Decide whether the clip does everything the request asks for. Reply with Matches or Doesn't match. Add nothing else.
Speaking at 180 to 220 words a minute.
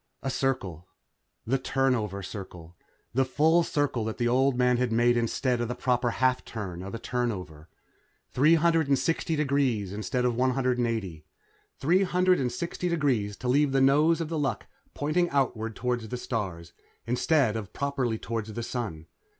Doesn't match